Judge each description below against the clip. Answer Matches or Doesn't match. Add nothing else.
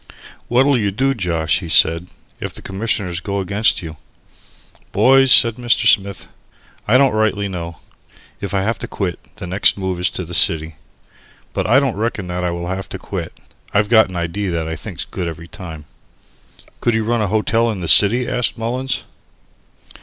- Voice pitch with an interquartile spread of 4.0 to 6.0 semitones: Matches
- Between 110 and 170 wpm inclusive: Doesn't match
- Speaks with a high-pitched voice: Doesn't match